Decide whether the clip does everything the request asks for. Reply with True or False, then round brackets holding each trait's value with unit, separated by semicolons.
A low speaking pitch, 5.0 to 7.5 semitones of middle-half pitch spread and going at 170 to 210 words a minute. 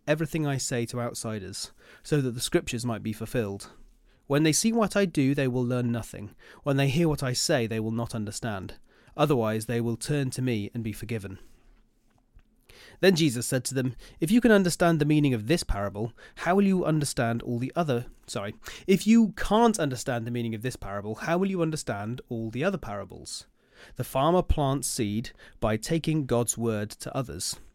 True (125 Hz; 5.4 semitones; 195 wpm)